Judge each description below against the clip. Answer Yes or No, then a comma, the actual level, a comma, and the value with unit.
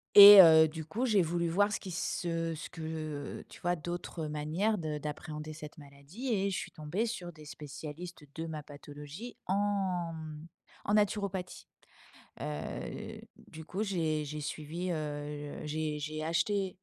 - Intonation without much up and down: No, average, 3.5 semitones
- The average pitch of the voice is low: No, medium, 160 Hz